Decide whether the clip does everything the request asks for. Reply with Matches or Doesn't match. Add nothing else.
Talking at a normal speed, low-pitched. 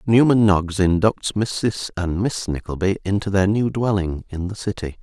Matches